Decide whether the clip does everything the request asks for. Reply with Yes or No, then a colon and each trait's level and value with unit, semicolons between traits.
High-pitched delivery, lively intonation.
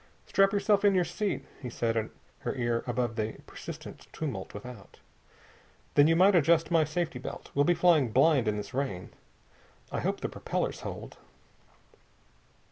No: medium, 140 Hz; wide, 6.9 semitones